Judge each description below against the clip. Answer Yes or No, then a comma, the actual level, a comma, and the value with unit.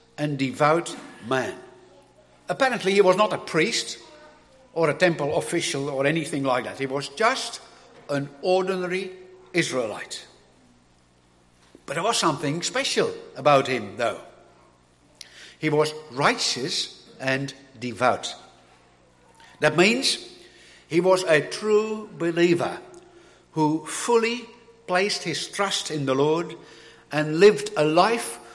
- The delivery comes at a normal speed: No, slow, 115 wpm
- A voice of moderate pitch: Yes, medium, 160 Hz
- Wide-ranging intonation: Yes, wide, 6.6 semitones